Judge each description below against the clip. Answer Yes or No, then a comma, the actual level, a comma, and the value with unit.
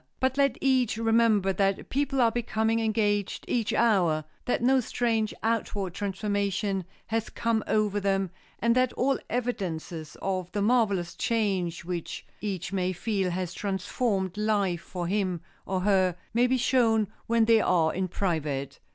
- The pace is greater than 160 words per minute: No, average, 150 wpm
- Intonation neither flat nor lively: Yes, average, 3.7 semitones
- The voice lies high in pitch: Yes, high, 205 Hz